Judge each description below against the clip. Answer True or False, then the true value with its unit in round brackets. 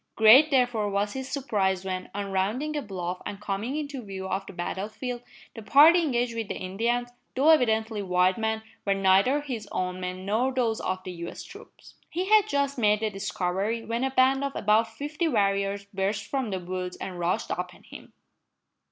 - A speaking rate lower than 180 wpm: False (190 wpm)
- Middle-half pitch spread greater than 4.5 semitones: True (5.2 semitones)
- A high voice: True (215 Hz)